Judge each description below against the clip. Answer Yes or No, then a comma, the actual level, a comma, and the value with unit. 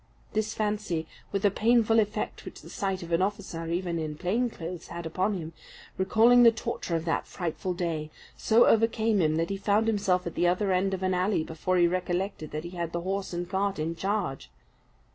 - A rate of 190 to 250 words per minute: Yes, fast, 205 wpm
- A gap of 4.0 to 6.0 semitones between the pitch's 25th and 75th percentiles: No, average, 3.4 semitones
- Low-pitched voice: No, medium, 185 Hz